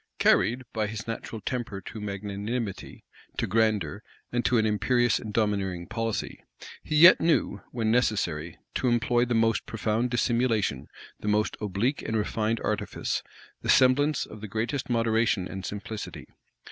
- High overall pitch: No, low, 110 Hz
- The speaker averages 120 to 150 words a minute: Yes, average, 145 wpm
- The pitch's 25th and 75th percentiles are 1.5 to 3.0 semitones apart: Yes, narrow, 2.6 semitones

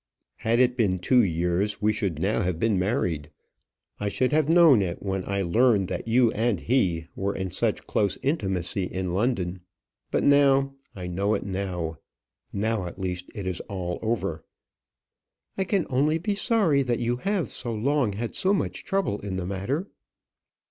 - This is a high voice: No, low, 105 Hz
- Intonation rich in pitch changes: Yes, wide, 5.7 semitones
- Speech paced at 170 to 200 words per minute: Yes, average, 175 wpm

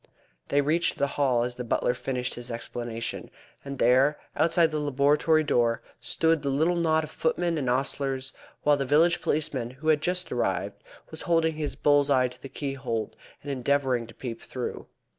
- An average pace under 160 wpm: No, average, 180 wpm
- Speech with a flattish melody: No, average, 3.7 semitones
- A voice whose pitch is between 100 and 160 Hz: Yes, medium, 140 Hz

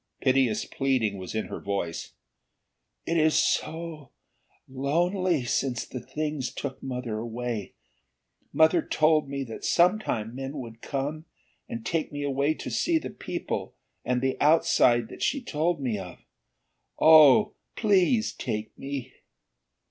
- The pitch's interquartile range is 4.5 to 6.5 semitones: Yes, average, 4.8 semitones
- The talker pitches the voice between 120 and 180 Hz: Yes, medium, 140 Hz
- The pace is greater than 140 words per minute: No, slow, 135 wpm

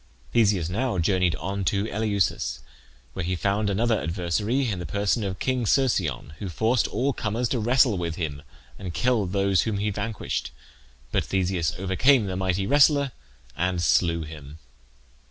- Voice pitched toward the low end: Yes, low, 100 Hz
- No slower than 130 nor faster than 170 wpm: Yes, average, 155 wpm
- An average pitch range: Yes, average, 4.2 semitones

